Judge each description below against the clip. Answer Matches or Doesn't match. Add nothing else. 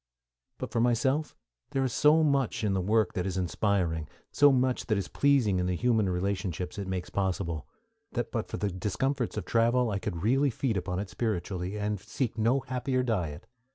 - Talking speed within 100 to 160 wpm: Doesn't match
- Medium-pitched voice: Doesn't match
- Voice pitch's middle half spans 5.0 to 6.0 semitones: Matches